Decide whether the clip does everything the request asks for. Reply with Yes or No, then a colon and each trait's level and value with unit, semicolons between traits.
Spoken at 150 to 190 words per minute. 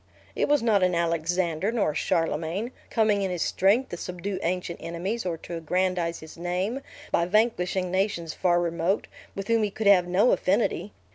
Yes: average, 180 wpm